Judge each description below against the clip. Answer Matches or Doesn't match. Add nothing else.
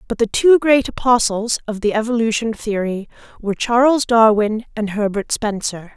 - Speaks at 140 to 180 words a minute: Matches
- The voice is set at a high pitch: Matches